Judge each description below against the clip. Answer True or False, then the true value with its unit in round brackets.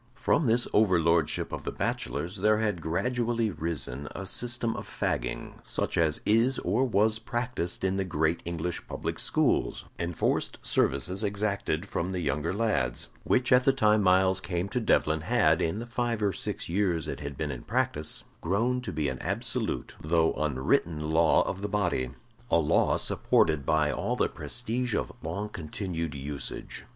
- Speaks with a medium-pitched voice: False (90 Hz)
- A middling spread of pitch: False (5.9 semitones)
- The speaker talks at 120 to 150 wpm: False (165 wpm)